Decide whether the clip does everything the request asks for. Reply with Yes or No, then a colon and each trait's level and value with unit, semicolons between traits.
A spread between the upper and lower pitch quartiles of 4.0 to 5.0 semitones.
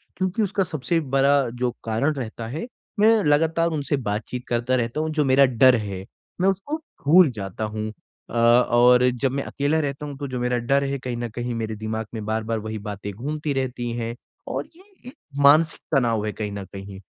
Yes: average, 4.5 semitones